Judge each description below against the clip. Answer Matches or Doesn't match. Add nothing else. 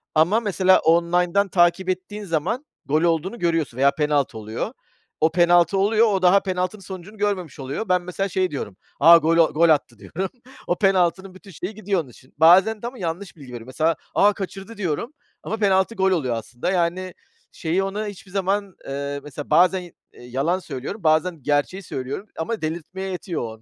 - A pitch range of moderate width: Matches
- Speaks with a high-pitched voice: Doesn't match